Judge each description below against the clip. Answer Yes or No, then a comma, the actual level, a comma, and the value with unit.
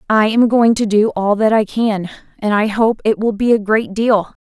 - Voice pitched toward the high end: Yes, high, 215 Hz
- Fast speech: Yes, fast, 245 wpm